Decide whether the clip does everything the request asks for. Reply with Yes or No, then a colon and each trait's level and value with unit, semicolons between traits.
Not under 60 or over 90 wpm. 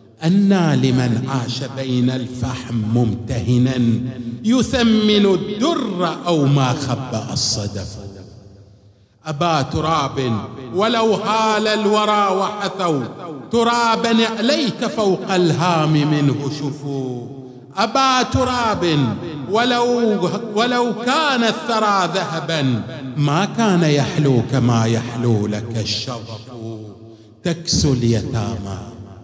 Yes: average, 80 wpm